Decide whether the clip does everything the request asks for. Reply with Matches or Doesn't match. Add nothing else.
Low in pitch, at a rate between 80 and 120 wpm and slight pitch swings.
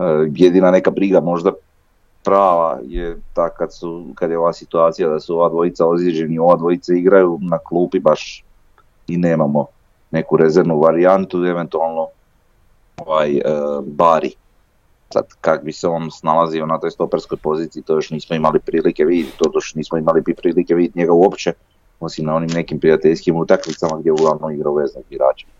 Doesn't match